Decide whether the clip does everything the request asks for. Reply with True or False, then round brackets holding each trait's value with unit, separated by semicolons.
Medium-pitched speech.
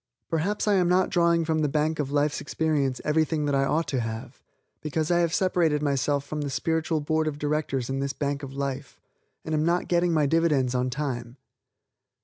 True (150 Hz)